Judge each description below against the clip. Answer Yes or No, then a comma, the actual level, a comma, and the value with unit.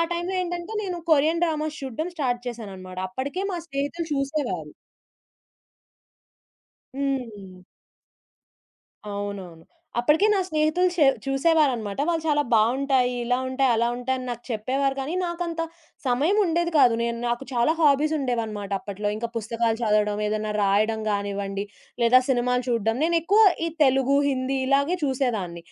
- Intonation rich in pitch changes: Yes, wide, 5.9 semitones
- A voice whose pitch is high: Yes, very high, 255 Hz